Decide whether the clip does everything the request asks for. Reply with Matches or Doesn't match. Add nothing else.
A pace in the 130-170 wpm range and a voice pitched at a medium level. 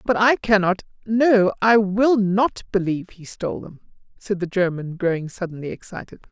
Doesn't match